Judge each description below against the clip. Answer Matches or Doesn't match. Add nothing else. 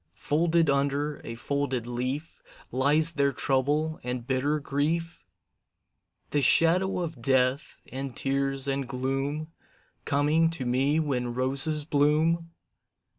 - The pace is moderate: Doesn't match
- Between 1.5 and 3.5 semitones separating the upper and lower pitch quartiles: Matches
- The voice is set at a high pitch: Doesn't match